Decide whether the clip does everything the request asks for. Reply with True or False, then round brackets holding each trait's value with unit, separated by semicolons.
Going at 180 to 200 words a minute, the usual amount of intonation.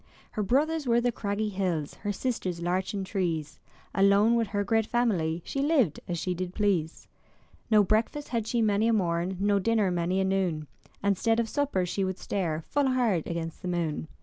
True (190 wpm; 4.3 semitones)